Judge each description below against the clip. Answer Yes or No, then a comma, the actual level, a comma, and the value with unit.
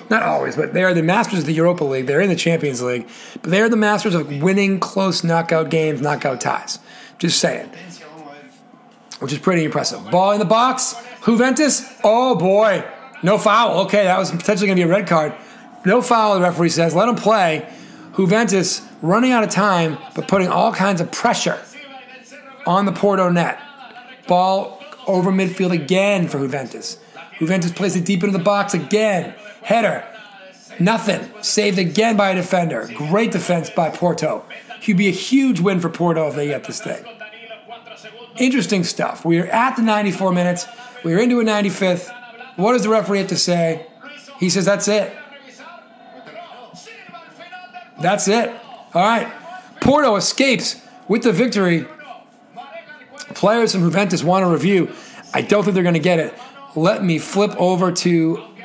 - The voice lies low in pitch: No, high, 200 Hz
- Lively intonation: No, average, 5.0 semitones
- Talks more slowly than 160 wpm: No, average, 170 wpm